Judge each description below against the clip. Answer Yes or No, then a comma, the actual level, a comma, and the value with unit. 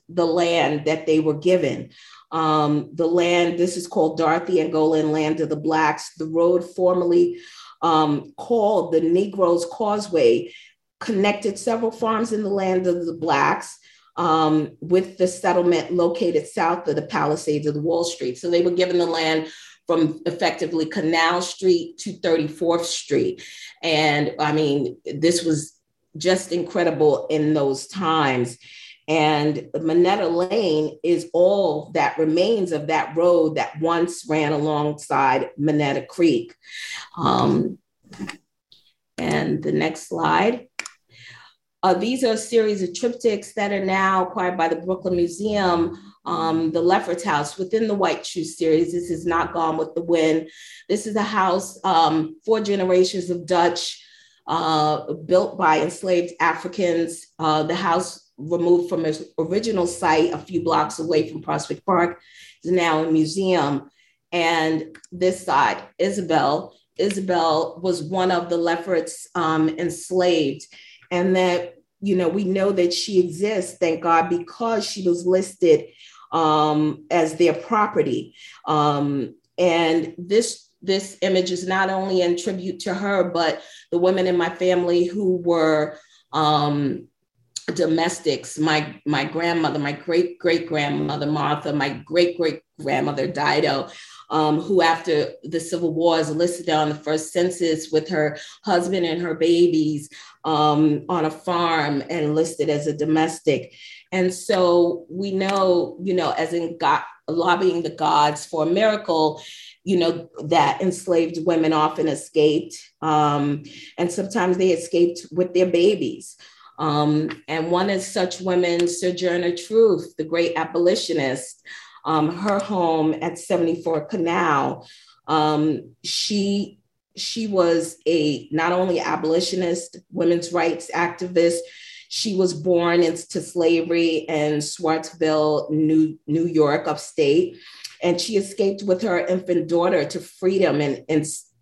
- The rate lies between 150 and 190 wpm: No, average, 140 wpm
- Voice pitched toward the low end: No, medium, 170 Hz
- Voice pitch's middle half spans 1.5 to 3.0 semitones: Yes, average, 2.7 semitones